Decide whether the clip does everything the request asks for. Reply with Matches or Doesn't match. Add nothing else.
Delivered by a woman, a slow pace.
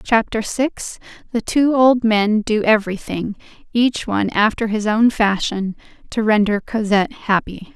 Matches